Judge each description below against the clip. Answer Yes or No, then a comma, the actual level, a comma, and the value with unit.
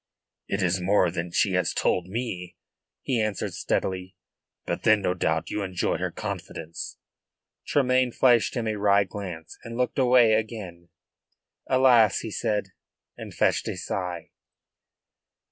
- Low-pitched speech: Yes, low, 100 Hz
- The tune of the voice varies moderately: Yes, average, 4.3 semitones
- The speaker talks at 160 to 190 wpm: No, average, 140 wpm